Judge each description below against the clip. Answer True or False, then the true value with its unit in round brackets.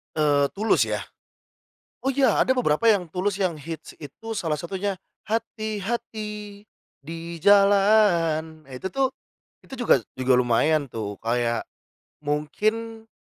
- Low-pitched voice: False (190 Hz)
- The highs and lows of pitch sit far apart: True (6.5 semitones)